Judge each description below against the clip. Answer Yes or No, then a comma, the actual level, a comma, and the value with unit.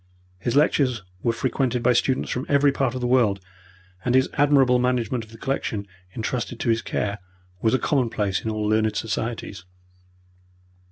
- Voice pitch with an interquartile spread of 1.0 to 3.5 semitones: Yes, average, 2.9 semitones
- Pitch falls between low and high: No, low, 120 Hz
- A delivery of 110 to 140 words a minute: No, average, 165 wpm